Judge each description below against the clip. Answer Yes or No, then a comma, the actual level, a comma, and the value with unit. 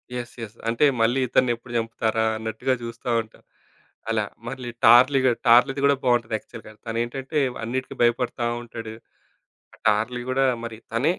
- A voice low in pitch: Yes, low, 120 Hz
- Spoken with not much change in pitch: Yes, narrow, 2.1 semitones